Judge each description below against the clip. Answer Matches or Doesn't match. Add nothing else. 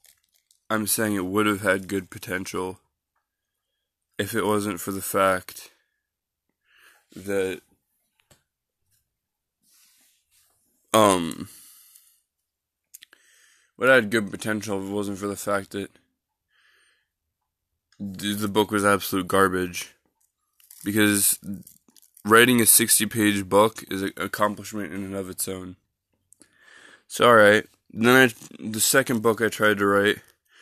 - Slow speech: Matches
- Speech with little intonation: Matches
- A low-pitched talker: Matches